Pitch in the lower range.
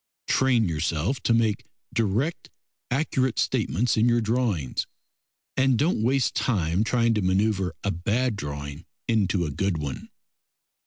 Yes: low, 110 Hz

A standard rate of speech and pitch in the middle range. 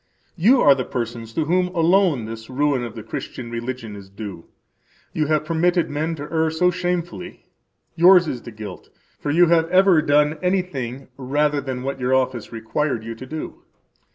Yes: average, 180 wpm; medium, 145 Hz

